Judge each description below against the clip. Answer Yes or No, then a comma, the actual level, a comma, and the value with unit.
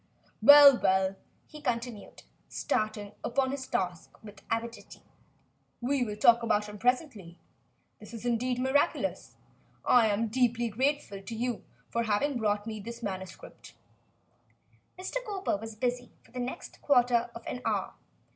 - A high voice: Yes, high, 235 Hz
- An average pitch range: Yes, average, 3.2 semitones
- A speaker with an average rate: Yes, average, 145 wpm